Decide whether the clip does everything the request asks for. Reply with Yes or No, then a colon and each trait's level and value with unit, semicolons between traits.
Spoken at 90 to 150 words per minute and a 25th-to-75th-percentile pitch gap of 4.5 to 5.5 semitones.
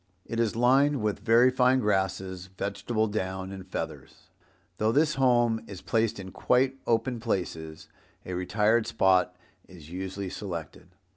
No: average, 140 wpm; average, 4.1 semitones